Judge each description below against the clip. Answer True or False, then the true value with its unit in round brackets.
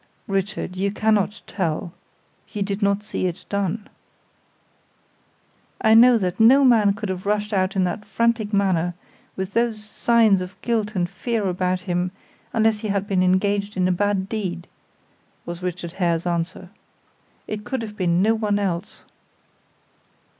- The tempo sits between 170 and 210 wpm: False (155 wpm)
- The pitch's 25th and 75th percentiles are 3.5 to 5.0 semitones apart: False (2.7 semitones)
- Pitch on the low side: False (200 Hz)